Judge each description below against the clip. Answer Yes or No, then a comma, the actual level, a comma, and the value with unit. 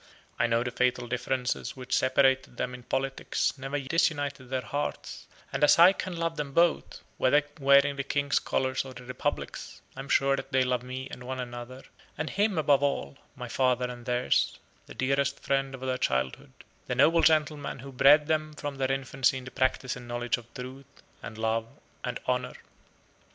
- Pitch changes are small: Yes, narrow, 2.1 semitones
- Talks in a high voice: No, low, 130 Hz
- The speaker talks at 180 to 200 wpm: Yes, average, 190 wpm